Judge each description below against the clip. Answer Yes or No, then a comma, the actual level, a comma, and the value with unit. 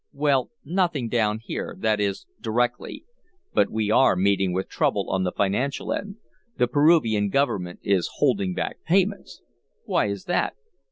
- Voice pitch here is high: No, low, 115 Hz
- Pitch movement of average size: No, wide, 6.8 semitones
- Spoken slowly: No, average, 150 wpm